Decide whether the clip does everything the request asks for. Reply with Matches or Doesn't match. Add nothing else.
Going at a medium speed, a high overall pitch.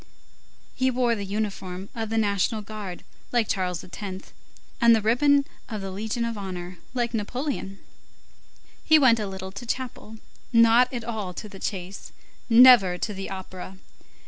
Matches